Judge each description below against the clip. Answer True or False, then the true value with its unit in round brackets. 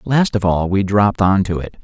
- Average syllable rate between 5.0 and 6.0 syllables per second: True (5.3 syllables/s)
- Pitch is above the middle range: False (100 Hz)